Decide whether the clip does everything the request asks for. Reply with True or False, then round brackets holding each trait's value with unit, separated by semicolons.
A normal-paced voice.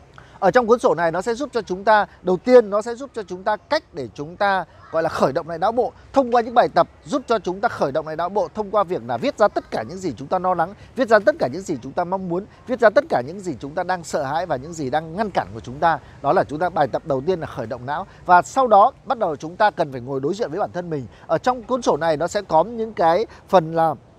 False (320 wpm)